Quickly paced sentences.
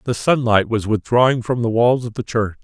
Yes: fast, 230 wpm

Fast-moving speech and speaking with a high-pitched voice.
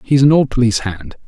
No: fast, 235 wpm; low, 120 Hz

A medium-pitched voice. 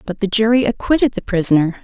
No: high, 210 Hz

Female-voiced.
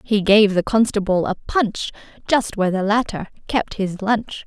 Yes: female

